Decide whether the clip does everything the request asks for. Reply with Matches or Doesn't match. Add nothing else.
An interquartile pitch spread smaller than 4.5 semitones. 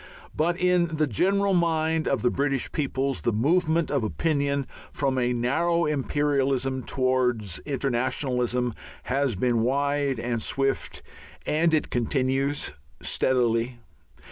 Matches